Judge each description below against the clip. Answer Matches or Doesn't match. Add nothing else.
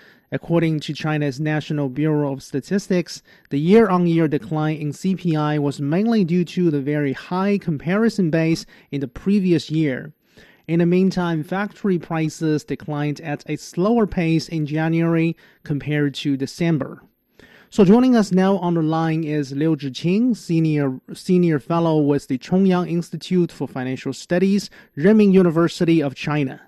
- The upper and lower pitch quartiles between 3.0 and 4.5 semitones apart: Matches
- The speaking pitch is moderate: Matches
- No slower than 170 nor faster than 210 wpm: Doesn't match